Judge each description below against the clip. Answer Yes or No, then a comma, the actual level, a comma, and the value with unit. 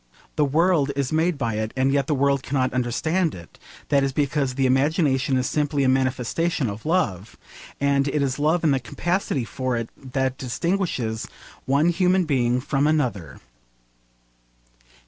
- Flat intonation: No, average, 3.3 semitones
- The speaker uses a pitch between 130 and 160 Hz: Yes, medium, 140 Hz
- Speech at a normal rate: Yes, average, 160 wpm